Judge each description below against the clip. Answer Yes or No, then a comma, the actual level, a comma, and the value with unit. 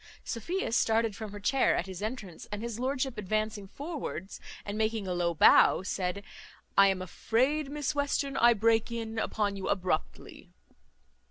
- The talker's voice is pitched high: Yes, high, 220 Hz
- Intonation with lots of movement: No, average, 4.3 semitones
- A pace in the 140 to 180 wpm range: Yes, average, 160 wpm